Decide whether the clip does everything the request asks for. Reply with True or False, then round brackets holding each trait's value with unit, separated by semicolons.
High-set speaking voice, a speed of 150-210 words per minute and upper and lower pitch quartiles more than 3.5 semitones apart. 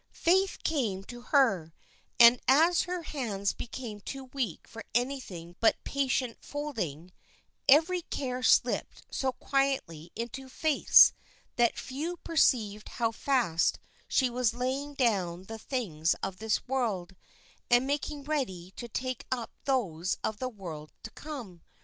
False (245 Hz; 135 wpm; 5.6 semitones)